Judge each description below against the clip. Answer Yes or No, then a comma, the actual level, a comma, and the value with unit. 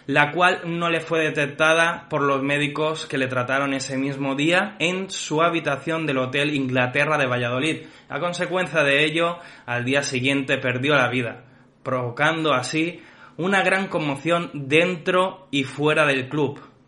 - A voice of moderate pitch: Yes, medium, 145 Hz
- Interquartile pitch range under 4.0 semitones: Yes, average, 3.6 semitones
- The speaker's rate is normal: Yes, average, 155 wpm